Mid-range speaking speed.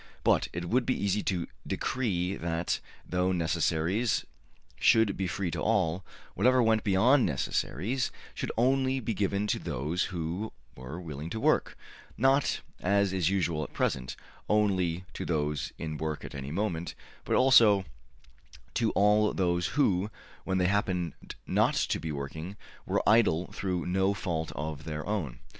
Yes: average, 150 wpm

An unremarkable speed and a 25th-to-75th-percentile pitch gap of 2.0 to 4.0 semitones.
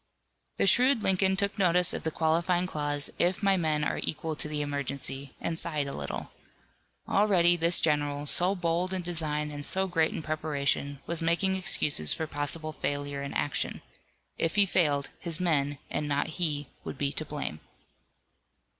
Yes: average, 170 wpm; average, 3.4 semitones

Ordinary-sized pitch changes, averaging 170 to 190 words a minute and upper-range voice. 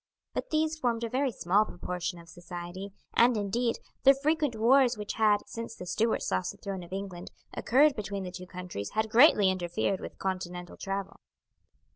Yes: average, 4.6 semitones; average, 175 wpm; high, 205 Hz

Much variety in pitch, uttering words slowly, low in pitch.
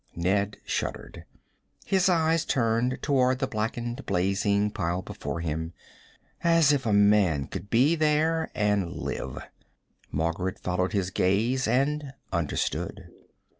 Yes: wide, 6.8 semitones; slow, 120 wpm; low, 105 Hz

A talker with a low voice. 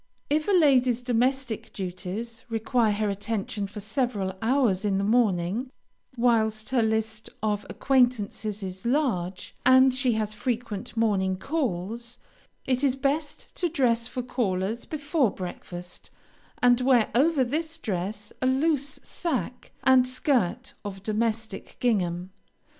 No: high, 230 Hz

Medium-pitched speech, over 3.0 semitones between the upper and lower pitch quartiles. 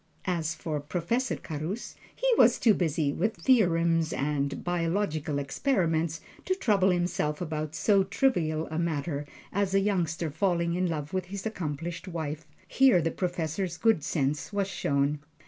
Yes: medium, 170 Hz; average, 3.8 semitones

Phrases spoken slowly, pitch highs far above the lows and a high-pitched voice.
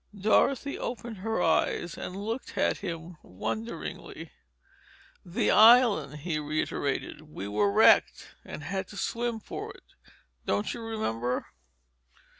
No: slow, 110 wpm; wide, 7.7 semitones; medium, 180 Hz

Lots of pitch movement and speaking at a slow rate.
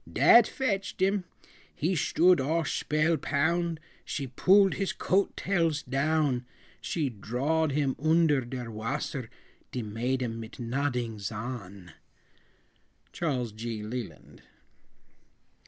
Yes: wide, 5.9 semitones; slow, 105 wpm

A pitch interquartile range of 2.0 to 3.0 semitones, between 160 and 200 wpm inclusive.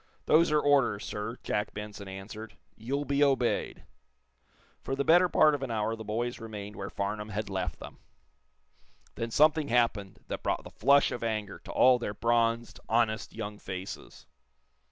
No: average, 4.4 semitones; average, 165 wpm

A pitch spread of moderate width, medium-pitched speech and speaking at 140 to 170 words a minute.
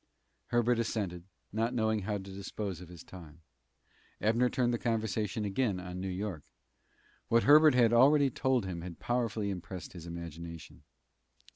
No: average, 4.7 semitones; low, 105 Hz; average, 150 wpm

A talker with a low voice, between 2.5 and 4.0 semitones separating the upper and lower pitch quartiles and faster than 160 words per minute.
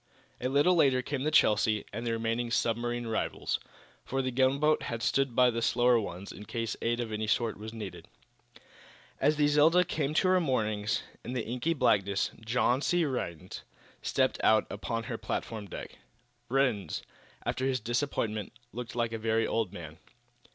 Yes: low, 120 Hz; average, 3.5 semitones; average, 170 wpm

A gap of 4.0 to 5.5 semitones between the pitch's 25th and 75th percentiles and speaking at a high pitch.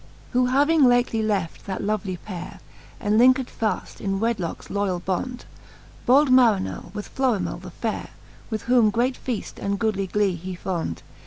Yes: average, 4.4 semitones; high, 215 Hz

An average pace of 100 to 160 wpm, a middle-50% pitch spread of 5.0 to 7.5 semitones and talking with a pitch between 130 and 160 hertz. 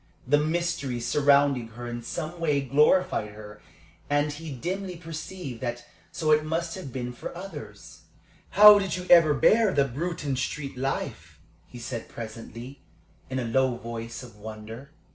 Yes: average, 155 wpm; wide, 5.5 semitones; medium, 140 Hz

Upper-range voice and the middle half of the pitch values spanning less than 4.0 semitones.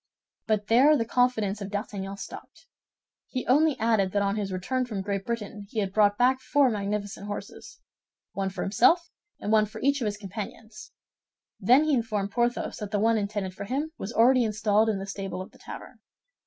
Yes: high, 215 Hz; average, 3.3 semitones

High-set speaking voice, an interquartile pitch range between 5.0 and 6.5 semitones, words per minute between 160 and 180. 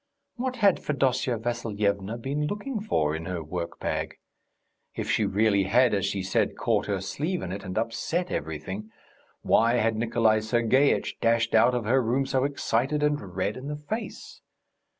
No: low, 115 Hz; wide, 5.5 semitones; average, 170 wpm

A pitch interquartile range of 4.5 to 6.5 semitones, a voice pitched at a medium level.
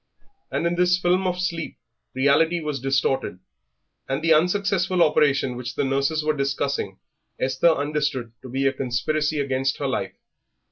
No: average, 3.9 semitones; medium, 145 Hz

